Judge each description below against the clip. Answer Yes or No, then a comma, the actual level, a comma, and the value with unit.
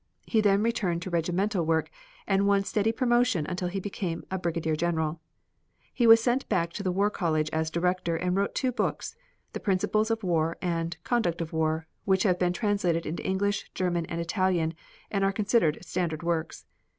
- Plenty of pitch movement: No, average, 3.4 semitones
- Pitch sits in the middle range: Yes, medium, 180 Hz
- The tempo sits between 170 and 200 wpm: Yes, average, 180 wpm